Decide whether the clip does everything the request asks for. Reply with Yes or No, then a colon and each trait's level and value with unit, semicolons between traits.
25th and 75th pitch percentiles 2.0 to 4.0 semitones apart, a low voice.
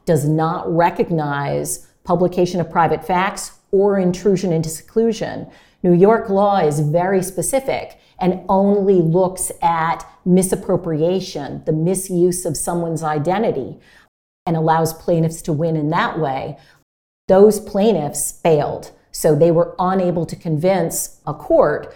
No: average, 2.9 semitones; medium, 175 Hz